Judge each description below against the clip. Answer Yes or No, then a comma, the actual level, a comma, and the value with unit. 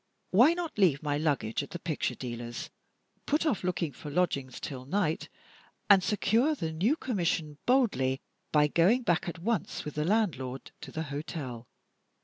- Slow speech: No, average, 160 wpm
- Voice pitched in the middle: Yes, medium, 165 Hz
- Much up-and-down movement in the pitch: Yes, wide, 6.6 semitones